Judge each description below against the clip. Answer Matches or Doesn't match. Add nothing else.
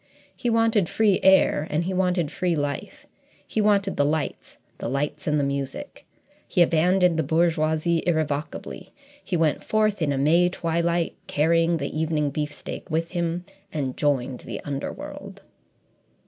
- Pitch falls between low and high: Matches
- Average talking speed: Matches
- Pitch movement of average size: Matches